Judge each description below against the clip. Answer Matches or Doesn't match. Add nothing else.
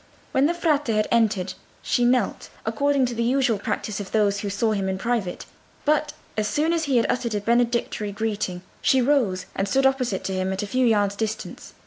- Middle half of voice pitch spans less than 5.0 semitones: Matches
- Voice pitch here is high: Matches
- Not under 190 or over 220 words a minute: Matches